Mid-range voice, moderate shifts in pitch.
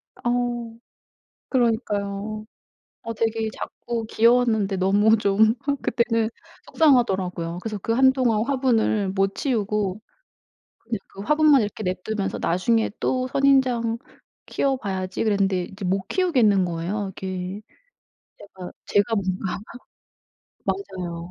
No: high, 215 Hz; average, 3.7 semitones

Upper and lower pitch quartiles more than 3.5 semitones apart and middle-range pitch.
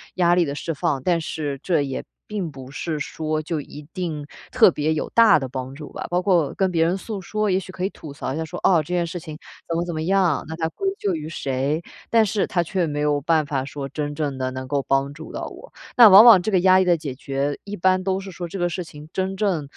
Yes: average, 4.2 semitones; medium, 165 Hz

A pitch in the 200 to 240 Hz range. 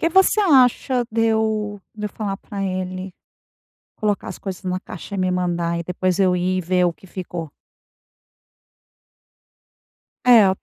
No: high, 190 Hz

